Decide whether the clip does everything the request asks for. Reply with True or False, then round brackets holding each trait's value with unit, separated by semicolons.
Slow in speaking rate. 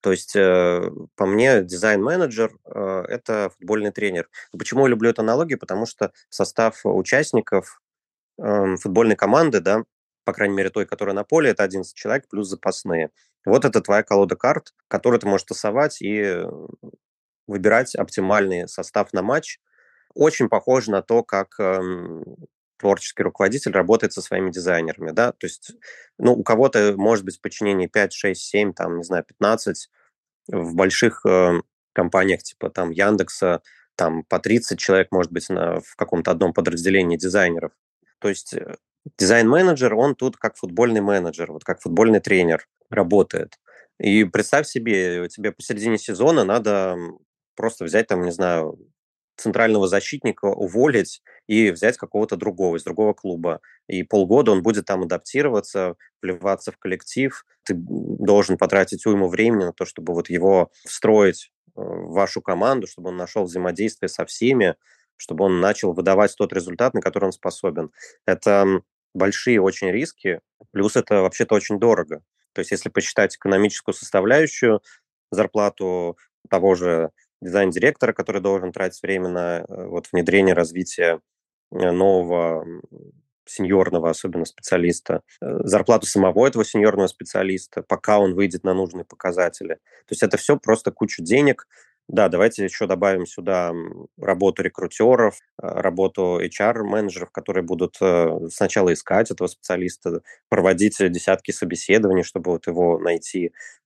False (140 wpm)